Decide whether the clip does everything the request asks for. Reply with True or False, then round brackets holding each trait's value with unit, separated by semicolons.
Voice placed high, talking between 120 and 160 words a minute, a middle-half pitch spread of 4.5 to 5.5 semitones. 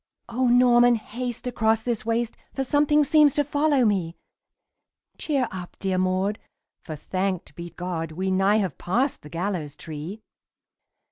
True (215 Hz; 145 wpm; 5.2 semitones)